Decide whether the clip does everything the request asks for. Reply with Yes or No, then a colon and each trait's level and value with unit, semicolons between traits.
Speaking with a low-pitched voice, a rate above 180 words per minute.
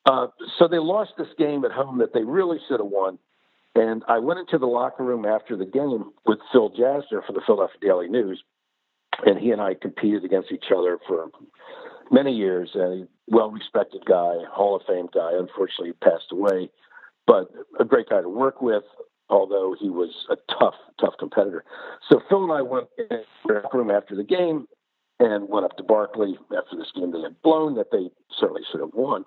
No: medium, 170 Hz; average, 200 wpm